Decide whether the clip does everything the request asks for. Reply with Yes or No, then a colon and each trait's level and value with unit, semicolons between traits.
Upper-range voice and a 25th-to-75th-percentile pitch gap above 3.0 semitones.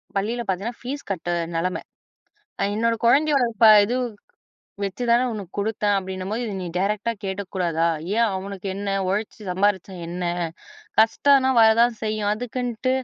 Yes: high, 210 Hz; average, 3.7 semitones